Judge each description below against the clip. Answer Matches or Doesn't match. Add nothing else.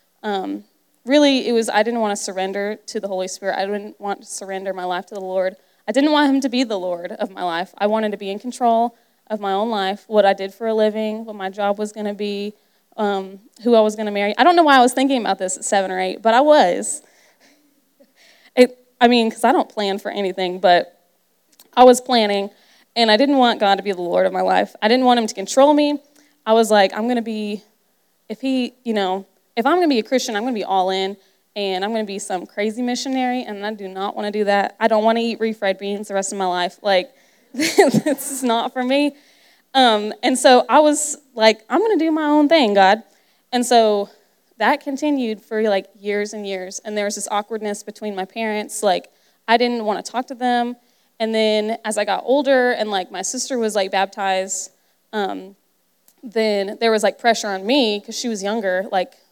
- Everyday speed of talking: Doesn't match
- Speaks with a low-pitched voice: Doesn't match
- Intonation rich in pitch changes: Doesn't match